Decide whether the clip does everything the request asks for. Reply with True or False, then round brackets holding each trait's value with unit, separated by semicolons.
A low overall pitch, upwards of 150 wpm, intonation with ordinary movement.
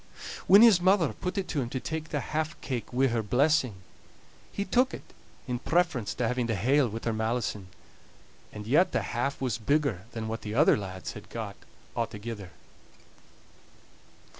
False (125 Hz; 170 wpm; 5.9 semitones)